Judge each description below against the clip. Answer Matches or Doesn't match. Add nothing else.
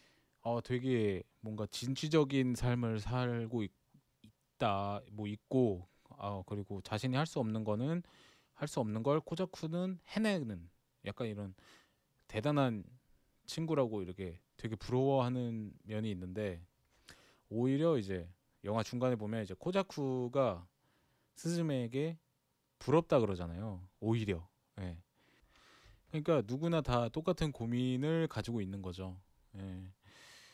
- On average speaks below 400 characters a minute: Matches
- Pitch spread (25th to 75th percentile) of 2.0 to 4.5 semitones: Doesn't match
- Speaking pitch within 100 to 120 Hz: Matches